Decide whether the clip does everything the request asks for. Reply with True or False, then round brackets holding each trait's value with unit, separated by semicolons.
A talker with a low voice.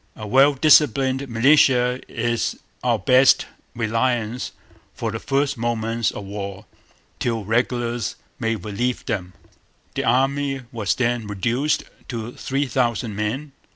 True (120 Hz)